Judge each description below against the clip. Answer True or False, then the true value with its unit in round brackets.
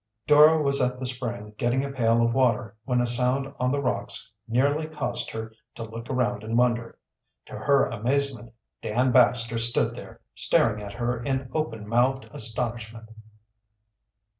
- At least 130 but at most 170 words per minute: True (160 wpm)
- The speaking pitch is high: False (120 Hz)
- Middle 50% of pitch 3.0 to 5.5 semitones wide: False (2.5 semitones)